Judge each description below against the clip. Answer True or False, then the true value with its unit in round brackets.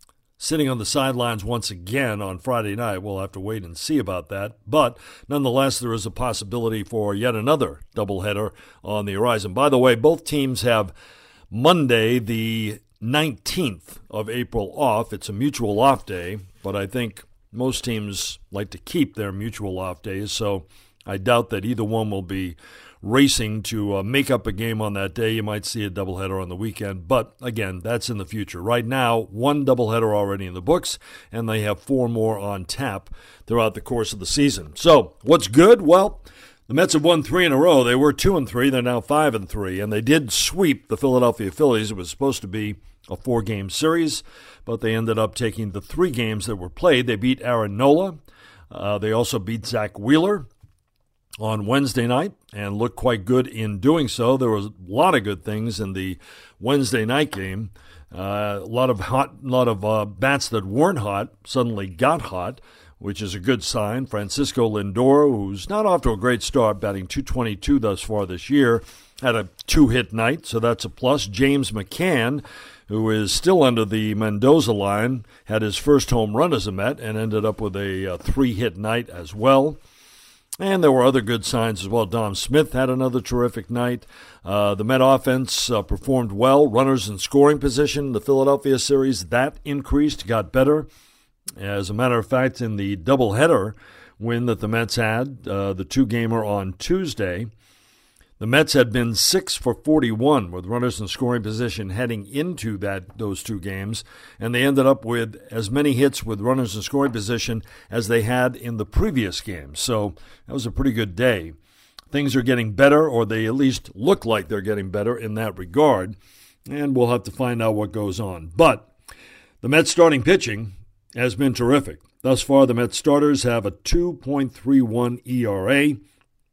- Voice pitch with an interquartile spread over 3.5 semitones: True (4.1 semitones)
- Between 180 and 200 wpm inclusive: True (190 wpm)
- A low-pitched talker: True (115 Hz)